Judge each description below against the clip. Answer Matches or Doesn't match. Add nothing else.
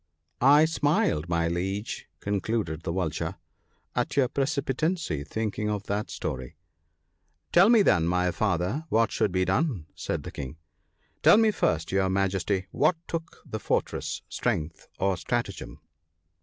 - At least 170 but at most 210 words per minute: Doesn't match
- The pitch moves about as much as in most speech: Doesn't match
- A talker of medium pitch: Doesn't match